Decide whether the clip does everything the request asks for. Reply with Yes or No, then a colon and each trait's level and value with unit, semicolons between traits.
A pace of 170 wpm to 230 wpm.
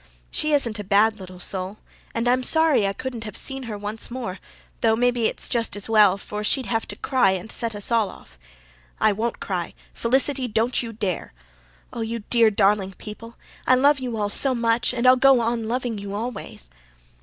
Yes: average, 195 wpm